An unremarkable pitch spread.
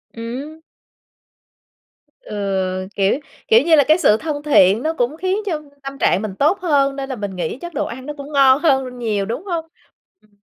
No: wide, 6.6 semitones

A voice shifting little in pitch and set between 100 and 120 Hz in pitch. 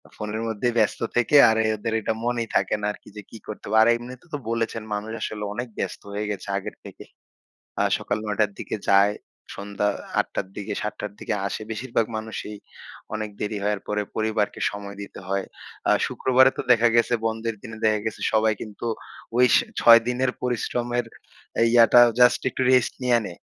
Yes: narrow, 2.3 semitones; low, 110 Hz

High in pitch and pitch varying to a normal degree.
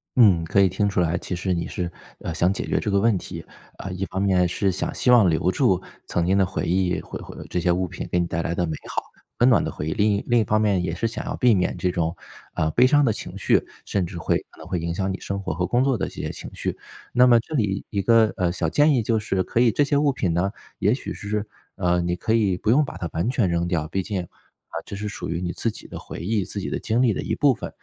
No: very low, 95 Hz; average, 4.2 semitones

